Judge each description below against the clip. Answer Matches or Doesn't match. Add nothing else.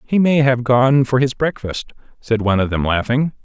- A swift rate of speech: Matches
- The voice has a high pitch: Doesn't match